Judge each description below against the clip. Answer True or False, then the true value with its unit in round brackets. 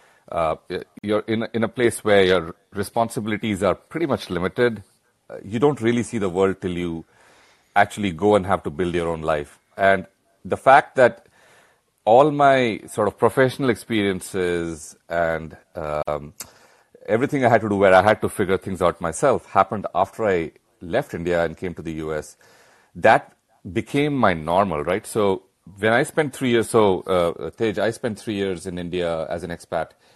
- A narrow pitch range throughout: False (4.7 semitones)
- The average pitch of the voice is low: True (100 Hz)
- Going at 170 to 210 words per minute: True (175 wpm)